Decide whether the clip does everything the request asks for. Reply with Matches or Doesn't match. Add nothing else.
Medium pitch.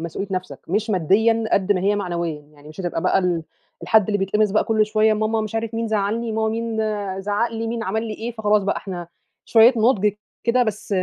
Doesn't match